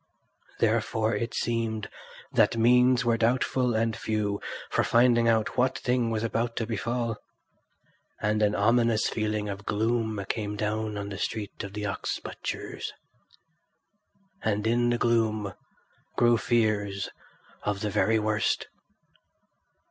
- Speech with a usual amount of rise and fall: No, narrow, 2.0 semitones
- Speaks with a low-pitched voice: Yes, low, 110 Hz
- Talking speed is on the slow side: Yes, slow, 130 wpm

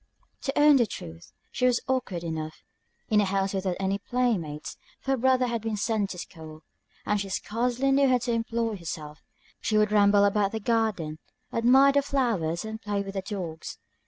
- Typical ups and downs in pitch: Yes, average, 4.4 semitones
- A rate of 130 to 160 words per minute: No, average, 190 wpm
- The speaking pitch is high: Yes, high, 210 Hz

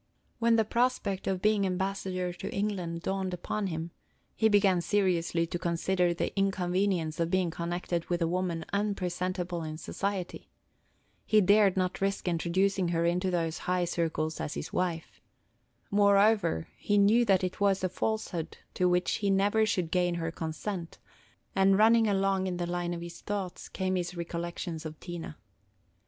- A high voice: No, medium, 180 Hz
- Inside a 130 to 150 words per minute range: No, average, 160 wpm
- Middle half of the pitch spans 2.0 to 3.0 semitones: Yes, narrow, 2.4 semitones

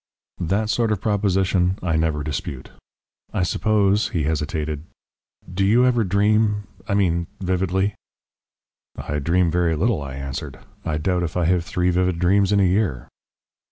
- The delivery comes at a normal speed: Yes, average, 155 wpm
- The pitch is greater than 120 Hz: No, very low, 90 Hz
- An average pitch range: Yes, average, 3.9 semitones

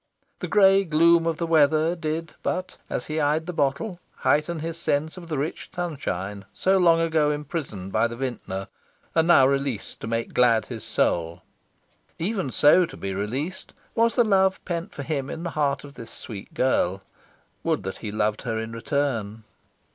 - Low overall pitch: No, medium, 150 Hz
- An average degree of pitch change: No, wide, 6.5 semitones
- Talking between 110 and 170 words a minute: No, average, 180 wpm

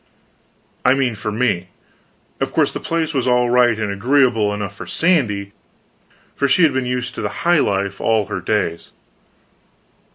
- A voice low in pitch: Yes, low, 120 Hz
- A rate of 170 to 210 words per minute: No, average, 160 wpm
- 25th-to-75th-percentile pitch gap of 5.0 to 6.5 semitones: No, average, 4.4 semitones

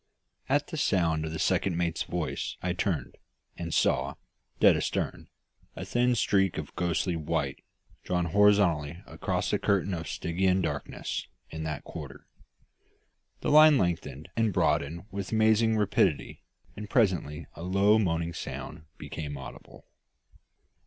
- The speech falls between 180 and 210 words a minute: No, slow, 135 wpm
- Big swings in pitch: No, average, 4.0 semitones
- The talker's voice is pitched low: Yes, very low, 90 Hz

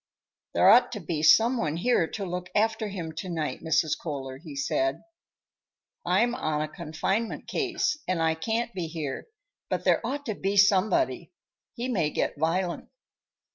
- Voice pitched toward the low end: No, medium, 185 Hz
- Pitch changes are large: Yes, wide, 6.2 semitones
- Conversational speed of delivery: Yes, average, 165 wpm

